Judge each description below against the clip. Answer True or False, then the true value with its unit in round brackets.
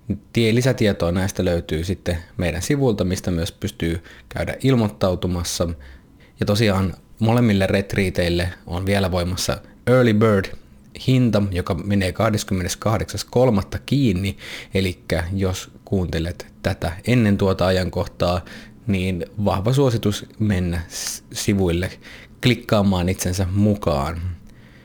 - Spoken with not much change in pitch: False (3.2 semitones)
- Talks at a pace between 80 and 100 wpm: True (95 wpm)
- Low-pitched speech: True (95 Hz)